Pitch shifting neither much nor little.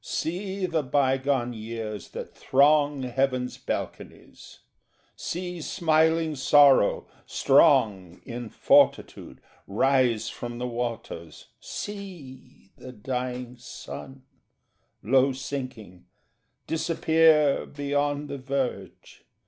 Yes: average, 3.4 semitones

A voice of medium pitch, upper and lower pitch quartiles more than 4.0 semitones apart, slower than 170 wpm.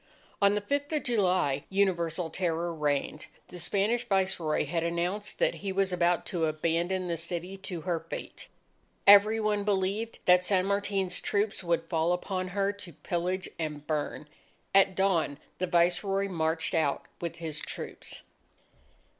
No: medium, 180 Hz; average, 3.0 semitones; average, 150 wpm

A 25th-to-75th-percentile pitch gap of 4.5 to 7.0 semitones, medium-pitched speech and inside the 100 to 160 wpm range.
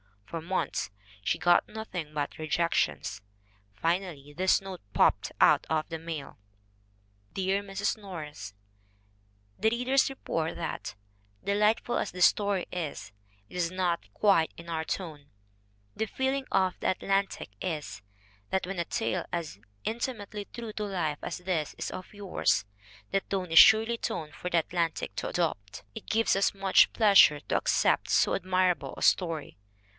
No: average, 3.8 semitones; medium, 180 Hz; average, 155 wpm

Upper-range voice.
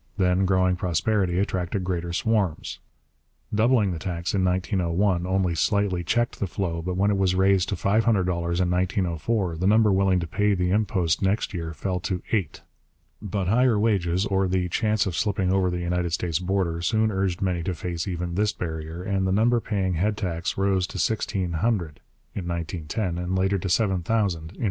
No: very low, 95 Hz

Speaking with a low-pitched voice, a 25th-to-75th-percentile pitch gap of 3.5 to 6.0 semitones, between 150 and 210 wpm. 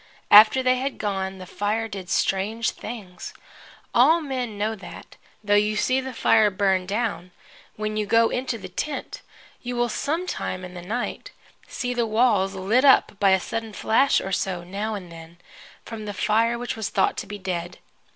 No: high, 215 Hz; average, 3.9 semitones; average, 185 wpm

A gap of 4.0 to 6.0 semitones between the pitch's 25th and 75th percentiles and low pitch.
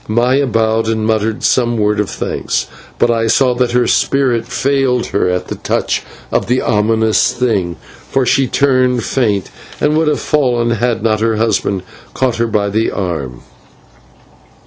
No: average, 2.8 semitones; low, 115 Hz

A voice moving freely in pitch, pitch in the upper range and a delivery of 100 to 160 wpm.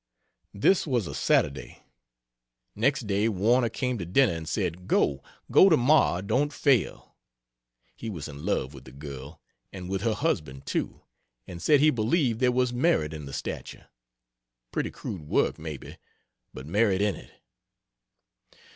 No: wide, 8.3 semitones; low, 100 Hz; average, 150 wpm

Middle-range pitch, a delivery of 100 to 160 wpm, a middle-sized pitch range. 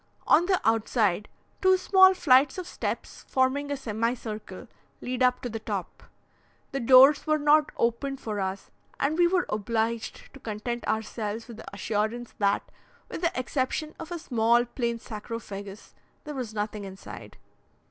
No: high, 240 Hz; average, 155 wpm; average, 4.7 semitones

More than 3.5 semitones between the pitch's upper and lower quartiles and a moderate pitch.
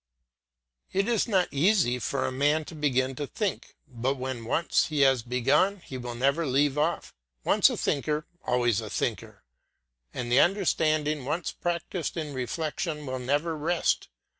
Yes: average, 4.3 semitones; medium, 145 Hz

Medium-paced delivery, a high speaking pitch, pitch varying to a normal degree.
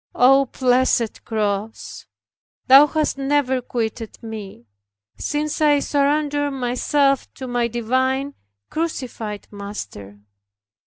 No: slow, 95 wpm; very high, 255 Hz; average, 4.2 semitones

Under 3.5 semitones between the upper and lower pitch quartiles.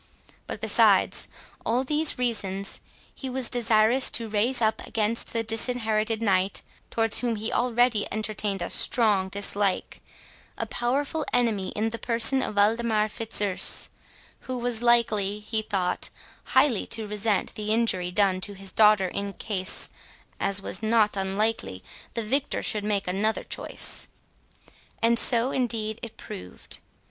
Yes: narrow, 2.6 semitones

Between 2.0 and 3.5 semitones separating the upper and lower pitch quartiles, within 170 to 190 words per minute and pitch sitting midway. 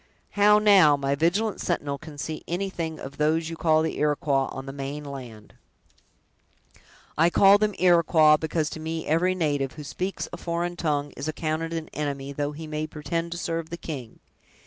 Yes: average, 2.8 semitones; average, 180 wpm; medium, 155 Hz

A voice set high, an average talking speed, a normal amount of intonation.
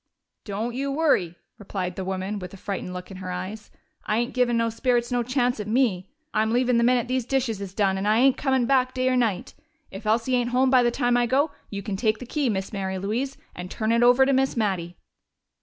No: high, 230 Hz; fast, 240 wpm; average, 4.4 semitones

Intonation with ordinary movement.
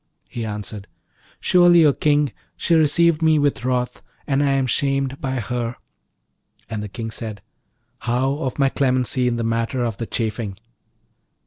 Yes: average, 3.8 semitones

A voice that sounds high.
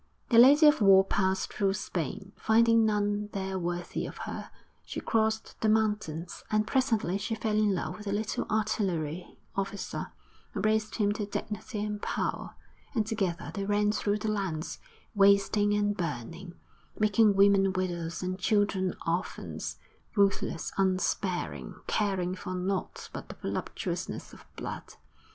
Yes: high, 200 Hz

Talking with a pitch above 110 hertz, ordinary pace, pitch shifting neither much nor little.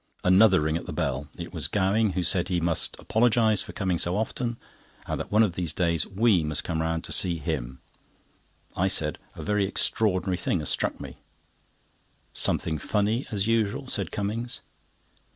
No: very low, 95 Hz; average, 170 wpm; average, 4.5 semitones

